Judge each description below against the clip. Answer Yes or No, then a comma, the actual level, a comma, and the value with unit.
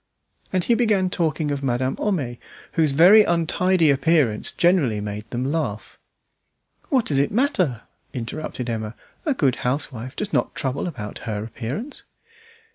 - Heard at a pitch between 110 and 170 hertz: Yes, medium, 140 Hz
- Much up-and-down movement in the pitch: Yes, wide, 7.0 semitones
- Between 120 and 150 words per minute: Yes, average, 140 wpm